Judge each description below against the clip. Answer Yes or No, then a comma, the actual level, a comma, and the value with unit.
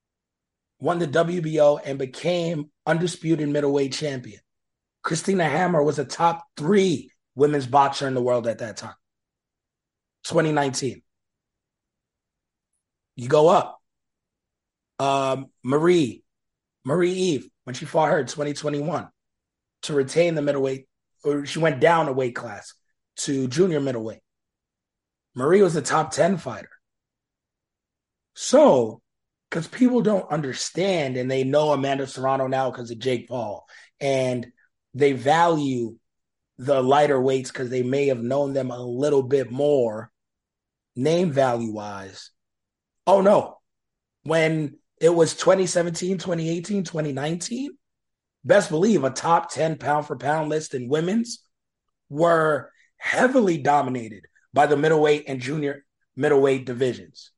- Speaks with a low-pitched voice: No, medium, 145 Hz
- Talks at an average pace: No, slow, 130 wpm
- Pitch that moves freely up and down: No, average, 3.7 semitones